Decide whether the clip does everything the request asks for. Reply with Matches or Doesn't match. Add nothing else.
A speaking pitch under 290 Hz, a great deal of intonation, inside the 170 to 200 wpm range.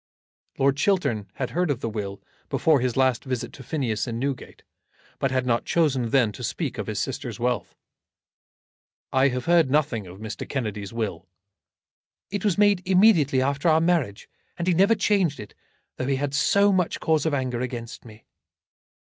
Matches